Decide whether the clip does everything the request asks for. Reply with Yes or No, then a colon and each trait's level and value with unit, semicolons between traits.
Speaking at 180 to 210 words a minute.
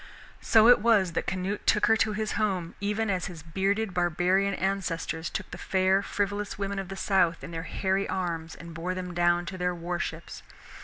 Yes: average, 200 wpm